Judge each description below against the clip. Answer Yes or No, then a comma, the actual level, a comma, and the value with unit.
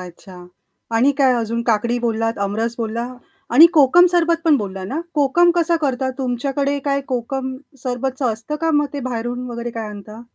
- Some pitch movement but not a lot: Yes, average, 3.8 semitones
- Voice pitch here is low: No, high, 245 Hz